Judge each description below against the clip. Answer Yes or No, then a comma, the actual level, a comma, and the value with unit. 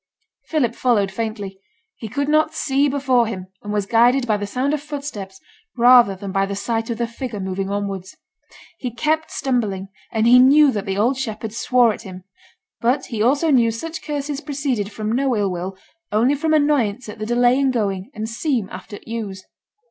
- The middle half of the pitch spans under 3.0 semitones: No, average, 4.9 semitones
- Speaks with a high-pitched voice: Yes, high, 230 Hz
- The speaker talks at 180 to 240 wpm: Yes, average, 195 wpm